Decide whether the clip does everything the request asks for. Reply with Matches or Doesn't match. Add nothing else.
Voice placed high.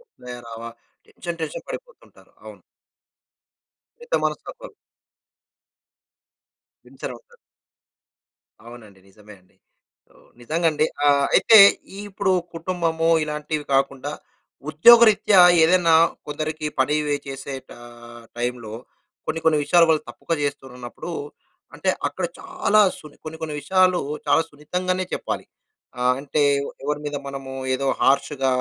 Doesn't match